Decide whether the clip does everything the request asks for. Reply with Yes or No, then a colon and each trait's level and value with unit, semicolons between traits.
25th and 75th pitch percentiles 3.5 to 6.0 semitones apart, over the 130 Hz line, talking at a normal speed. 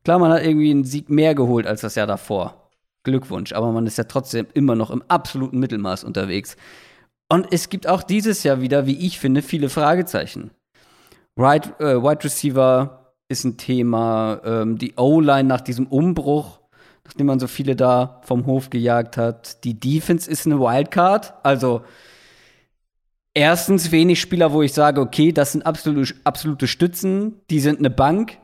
Yes: average, 4.1 semitones; medium, 140 Hz; average, 165 wpm